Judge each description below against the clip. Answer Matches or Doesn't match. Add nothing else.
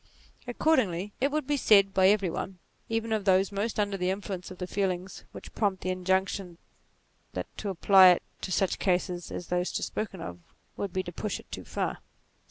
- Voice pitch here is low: Doesn't match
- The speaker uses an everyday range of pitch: Doesn't match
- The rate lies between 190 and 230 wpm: Matches